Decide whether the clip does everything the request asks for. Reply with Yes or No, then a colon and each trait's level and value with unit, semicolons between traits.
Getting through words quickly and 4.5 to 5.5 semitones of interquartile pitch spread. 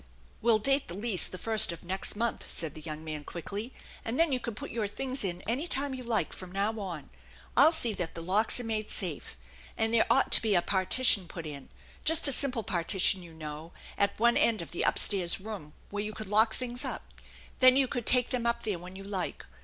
Yes: fast, 235 wpm; average, 5.0 semitones